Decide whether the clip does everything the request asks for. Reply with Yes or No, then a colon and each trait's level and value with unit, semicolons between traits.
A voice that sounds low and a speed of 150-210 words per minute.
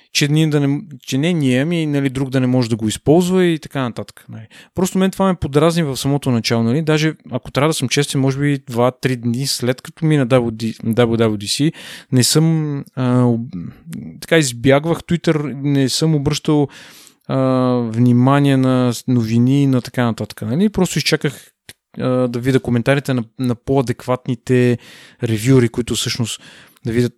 Yes: low, 130 Hz; fast, 165 wpm